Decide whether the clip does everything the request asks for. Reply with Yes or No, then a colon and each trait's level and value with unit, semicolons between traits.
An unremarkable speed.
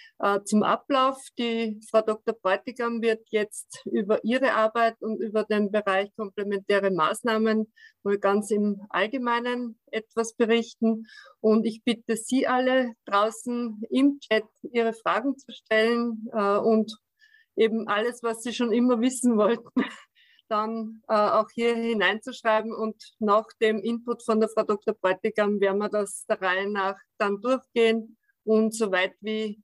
Yes: average, 140 wpm